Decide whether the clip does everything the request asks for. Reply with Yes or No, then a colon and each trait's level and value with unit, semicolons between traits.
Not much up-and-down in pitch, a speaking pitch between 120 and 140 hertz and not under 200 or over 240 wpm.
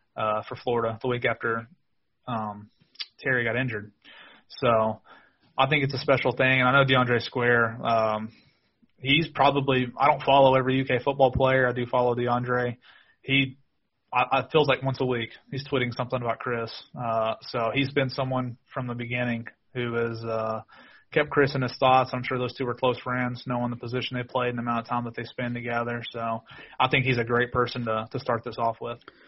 Yes: narrow, 2.0 semitones; low, 125 Hz; fast, 205 wpm